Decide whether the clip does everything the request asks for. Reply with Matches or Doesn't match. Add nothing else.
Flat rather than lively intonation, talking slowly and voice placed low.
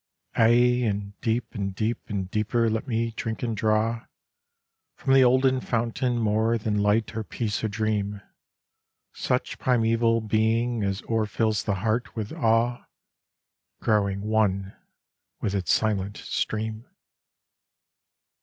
Matches